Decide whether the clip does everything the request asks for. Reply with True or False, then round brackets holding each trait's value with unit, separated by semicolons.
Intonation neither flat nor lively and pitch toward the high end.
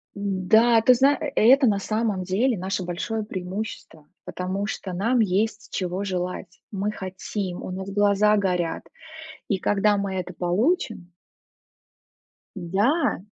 True (3.0 semitones; 200 Hz)